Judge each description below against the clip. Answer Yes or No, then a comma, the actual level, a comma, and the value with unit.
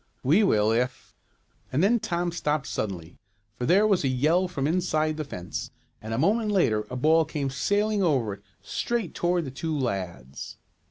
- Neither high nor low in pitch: Yes, medium, 150 Hz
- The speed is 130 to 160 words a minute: No, average, 180 wpm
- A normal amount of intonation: No, wide, 6.5 semitones